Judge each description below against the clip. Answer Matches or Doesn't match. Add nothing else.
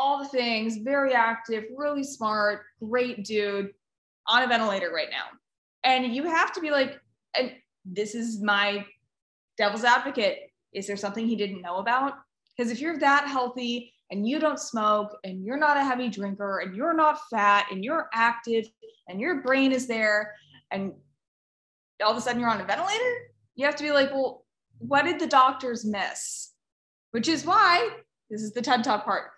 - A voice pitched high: Matches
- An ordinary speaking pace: Matches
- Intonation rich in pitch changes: Doesn't match